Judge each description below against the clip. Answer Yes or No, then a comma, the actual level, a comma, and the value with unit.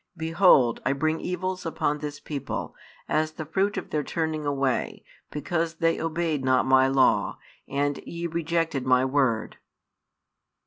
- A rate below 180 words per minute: Yes, average, 140 wpm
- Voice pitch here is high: No, medium, 155 Hz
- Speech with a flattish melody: No, average, 3.4 semitones